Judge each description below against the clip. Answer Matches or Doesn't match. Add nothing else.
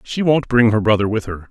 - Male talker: Matches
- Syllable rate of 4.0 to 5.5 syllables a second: Doesn't match